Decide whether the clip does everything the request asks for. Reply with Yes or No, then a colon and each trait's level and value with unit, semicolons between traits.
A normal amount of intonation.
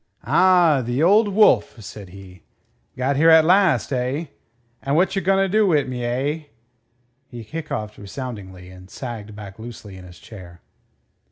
No: wide, 8.0 semitones